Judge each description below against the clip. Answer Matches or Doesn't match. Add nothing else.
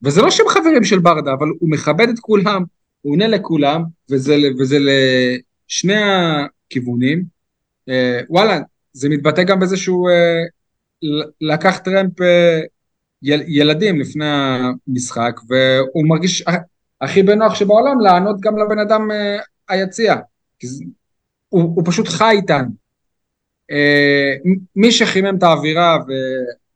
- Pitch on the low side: Doesn't match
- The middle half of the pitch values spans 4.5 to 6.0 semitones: Matches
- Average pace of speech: Matches